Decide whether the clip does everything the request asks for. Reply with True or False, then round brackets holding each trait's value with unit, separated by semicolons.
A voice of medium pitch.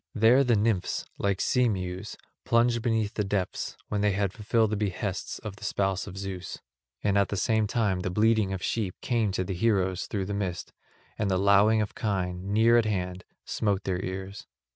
False (100 Hz)